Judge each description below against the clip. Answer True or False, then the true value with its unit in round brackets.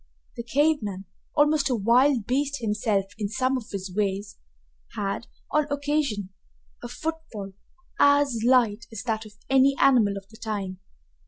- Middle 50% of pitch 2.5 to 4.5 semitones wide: False (5.3 semitones)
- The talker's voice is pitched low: False (230 Hz)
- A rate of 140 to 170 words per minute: True (150 wpm)